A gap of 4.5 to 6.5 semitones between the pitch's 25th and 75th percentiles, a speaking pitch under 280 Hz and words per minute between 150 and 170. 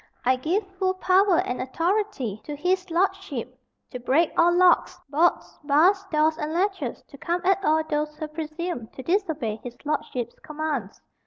No: average, 4.8 semitones; very high, 315 Hz; average, 160 wpm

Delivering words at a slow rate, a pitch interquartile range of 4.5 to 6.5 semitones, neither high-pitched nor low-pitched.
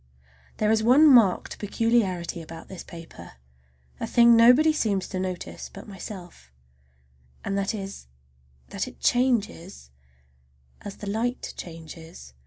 No: slow, 125 wpm; average, 5.0 semitones; high, 200 Hz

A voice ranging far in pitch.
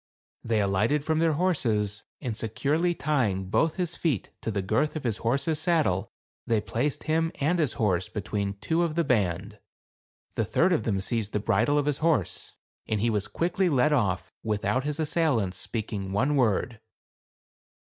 Yes: wide, 6.9 semitones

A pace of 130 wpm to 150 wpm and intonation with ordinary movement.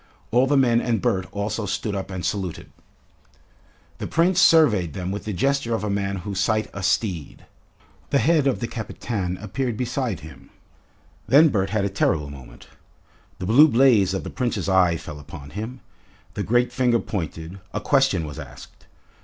No: average, 175 wpm; average, 4.9 semitones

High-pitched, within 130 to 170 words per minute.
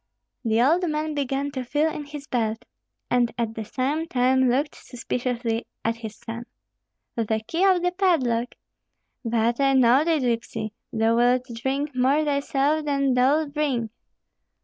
Yes: very high, 260 Hz; average, 150 wpm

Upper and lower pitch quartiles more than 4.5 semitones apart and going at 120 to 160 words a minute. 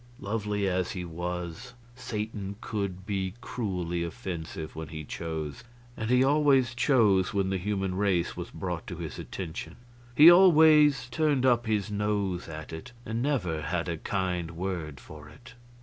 Yes: wide, 5.5 semitones; average, 155 wpm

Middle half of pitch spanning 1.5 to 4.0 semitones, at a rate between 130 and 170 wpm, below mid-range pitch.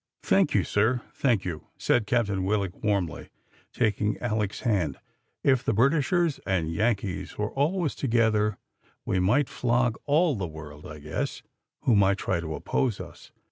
No: average, 4.7 semitones; average, 150 wpm; low, 105 Hz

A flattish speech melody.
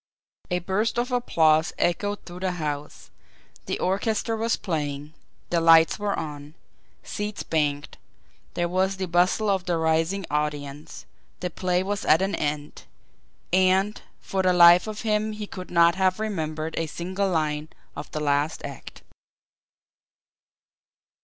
No: average, 3.9 semitones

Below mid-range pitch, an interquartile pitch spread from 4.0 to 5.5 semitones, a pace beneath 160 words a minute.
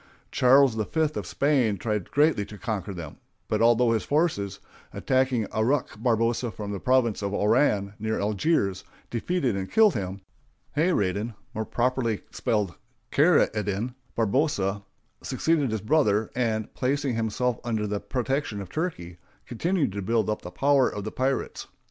Yes: low, 115 Hz; average, 4.6 semitones; average, 150 wpm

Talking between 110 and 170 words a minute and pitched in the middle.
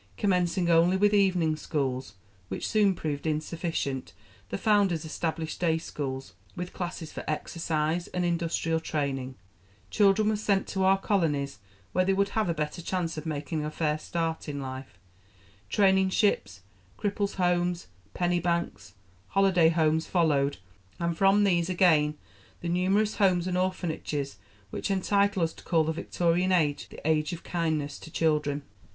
Yes: average, 150 wpm; medium, 170 Hz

